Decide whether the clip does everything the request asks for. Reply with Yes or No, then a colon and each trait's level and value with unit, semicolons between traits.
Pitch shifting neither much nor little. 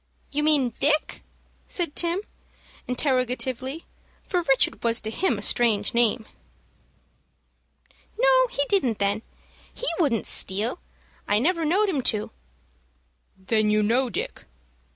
No: wide, 6.7 semitones